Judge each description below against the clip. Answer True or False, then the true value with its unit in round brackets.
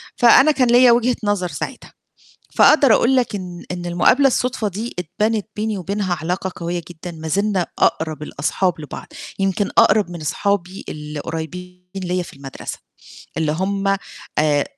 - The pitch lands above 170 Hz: True (185 Hz)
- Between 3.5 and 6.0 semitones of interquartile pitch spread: True (4.2 semitones)